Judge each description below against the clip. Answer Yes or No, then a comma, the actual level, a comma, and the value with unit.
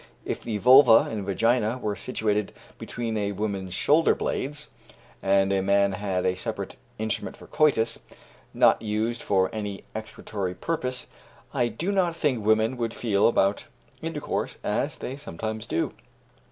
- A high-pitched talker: No, low, 110 Hz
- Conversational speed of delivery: Yes, average, 145 wpm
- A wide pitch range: No, average, 3.5 semitones